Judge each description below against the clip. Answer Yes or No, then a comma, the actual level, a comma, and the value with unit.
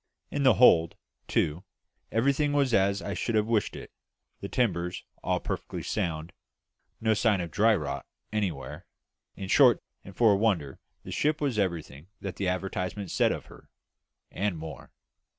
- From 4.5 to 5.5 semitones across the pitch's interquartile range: Yes, average, 4.8 semitones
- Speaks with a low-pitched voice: Yes, low, 100 Hz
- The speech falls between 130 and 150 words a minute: No, average, 160 wpm